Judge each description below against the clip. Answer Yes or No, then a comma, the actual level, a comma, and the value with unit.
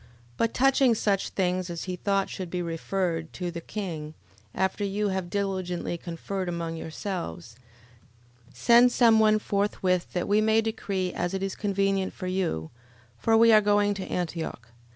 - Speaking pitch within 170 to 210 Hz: Yes, high, 190 Hz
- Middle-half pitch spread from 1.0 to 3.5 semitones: Yes, average, 2.9 semitones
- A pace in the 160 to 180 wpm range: Yes, average, 165 wpm